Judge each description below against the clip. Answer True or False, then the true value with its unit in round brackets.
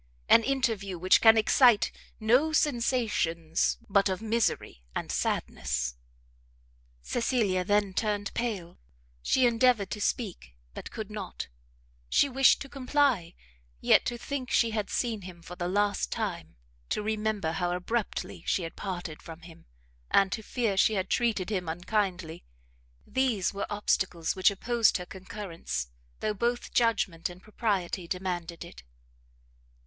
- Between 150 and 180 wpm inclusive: False (140 wpm)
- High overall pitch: True (205 Hz)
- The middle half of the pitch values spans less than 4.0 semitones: False (4.5 semitones)